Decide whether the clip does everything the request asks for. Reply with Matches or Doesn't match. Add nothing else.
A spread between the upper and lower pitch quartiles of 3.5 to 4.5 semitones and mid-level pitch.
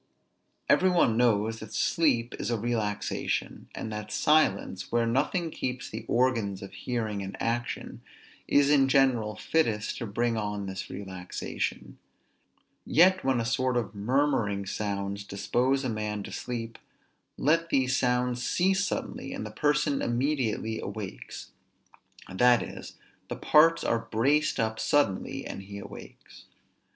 Doesn't match